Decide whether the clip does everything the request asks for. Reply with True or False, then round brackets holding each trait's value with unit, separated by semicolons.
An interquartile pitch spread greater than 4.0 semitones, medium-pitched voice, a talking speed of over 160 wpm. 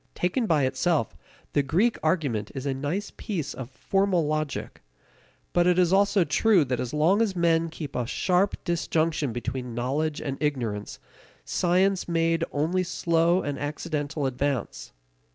False (4.5 semitones; 160 Hz; 150 wpm)